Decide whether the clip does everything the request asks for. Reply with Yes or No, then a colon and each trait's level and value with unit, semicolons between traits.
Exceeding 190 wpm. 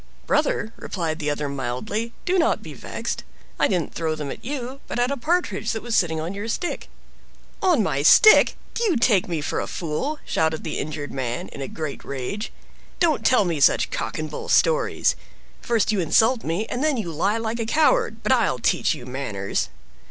Yes: average, 200 wpm